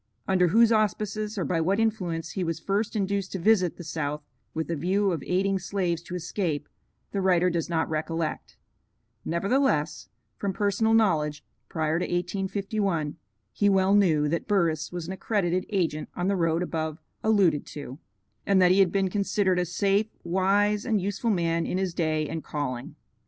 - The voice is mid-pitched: Yes, medium, 180 Hz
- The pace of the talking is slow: No, average, 175 wpm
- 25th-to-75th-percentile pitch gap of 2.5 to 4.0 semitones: Yes, average, 3.4 semitones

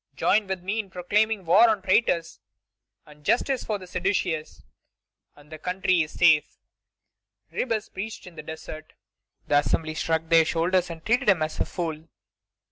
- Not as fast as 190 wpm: Yes, average, 160 wpm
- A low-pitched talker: No, medium, 180 Hz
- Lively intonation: No, average, 4.2 semitones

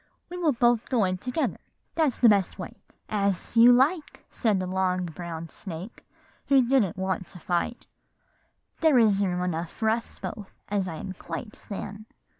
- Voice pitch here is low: No, high, 205 Hz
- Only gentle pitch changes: No, average, 4.7 semitones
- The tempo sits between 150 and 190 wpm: Yes, average, 170 wpm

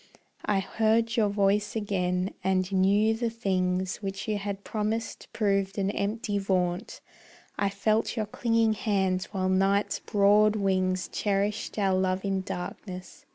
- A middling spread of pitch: No, narrow, 2.0 semitones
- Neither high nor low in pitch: No, high, 200 Hz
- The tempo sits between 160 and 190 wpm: No, average, 140 wpm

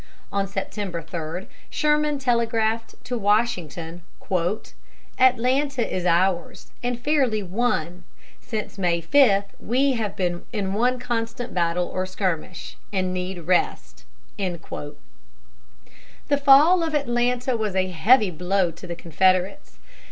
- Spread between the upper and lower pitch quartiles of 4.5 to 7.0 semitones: Yes, wide, 5.6 semitones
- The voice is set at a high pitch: Yes, high, 205 Hz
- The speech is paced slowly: Yes, slow, 115 wpm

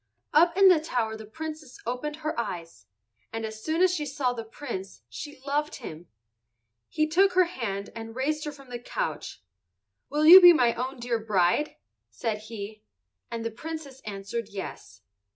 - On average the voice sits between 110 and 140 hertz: No, high, 245 Hz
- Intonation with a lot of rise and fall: Yes, wide, 6.0 semitones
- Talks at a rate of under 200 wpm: Yes, average, 170 wpm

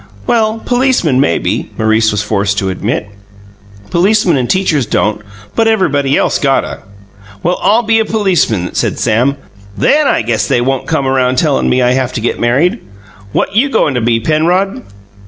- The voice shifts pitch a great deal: Yes, wide, 8.7 semitones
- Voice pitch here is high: No, low, 135 Hz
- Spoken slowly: No, average, 170 wpm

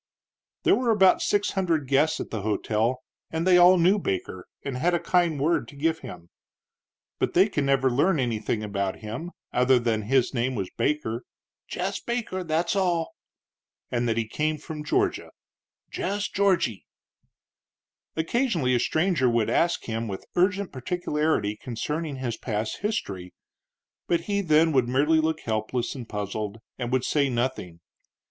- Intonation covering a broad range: Yes, wide, 6.8 semitones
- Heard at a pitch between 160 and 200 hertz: No, medium, 140 Hz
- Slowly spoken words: No, average, 155 wpm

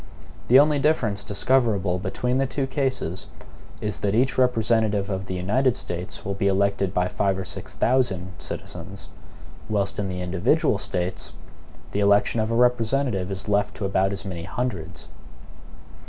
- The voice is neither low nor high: No, low, 100 Hz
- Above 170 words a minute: No, average, 155 wpm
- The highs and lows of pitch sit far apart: No, average, 4.5 semitones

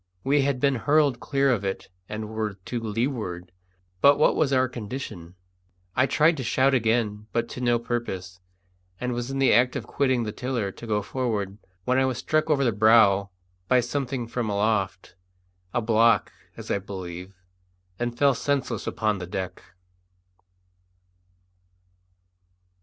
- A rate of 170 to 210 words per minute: No, average, 155 wpm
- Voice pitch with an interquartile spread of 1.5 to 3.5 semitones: No, average, 4.1 semitones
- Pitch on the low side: Yes, low, 120 Hz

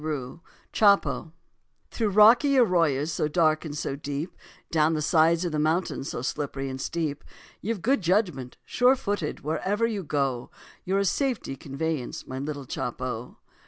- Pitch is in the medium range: Yes, medium, 160 Hz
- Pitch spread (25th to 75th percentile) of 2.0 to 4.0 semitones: No, wide, 5.6 semitones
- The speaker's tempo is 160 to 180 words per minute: No, average, 150 wpm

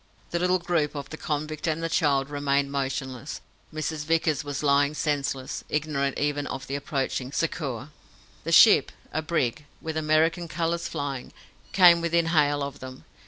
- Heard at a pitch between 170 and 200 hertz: No, medium, 150 Hz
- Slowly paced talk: No, average, 160 wpm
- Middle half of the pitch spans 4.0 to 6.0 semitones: No, narrow, 2.5 semitones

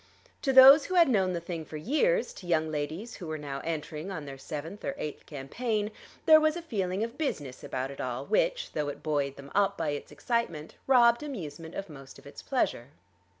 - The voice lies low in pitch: No, medium, 170 Hz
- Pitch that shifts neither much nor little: No, wide, 8.7 semitones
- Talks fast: Yes, fast, 210 wpm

